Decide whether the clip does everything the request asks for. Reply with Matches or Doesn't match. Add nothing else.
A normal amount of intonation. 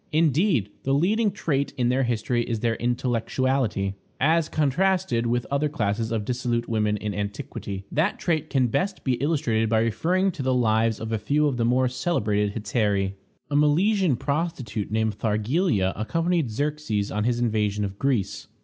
Doesn't match